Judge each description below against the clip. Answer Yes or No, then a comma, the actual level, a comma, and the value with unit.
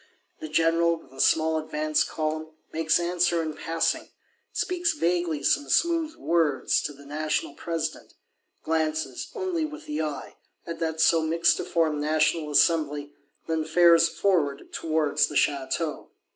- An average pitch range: No, narrow, 1.8 semitones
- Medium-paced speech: No, slow, 130 wpm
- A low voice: No, medium, 160 Hz